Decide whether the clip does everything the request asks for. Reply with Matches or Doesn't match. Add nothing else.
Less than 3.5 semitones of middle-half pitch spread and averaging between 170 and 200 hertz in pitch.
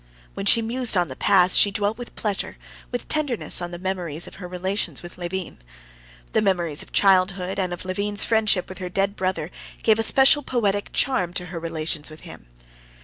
Matches